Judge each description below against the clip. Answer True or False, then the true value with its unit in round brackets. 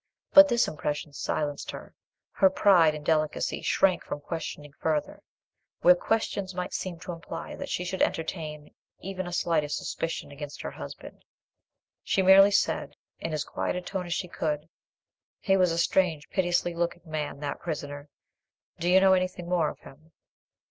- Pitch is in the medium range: True (170 Hz)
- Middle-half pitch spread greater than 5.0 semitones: False (3.4 semitones)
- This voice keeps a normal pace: True (165 wpm)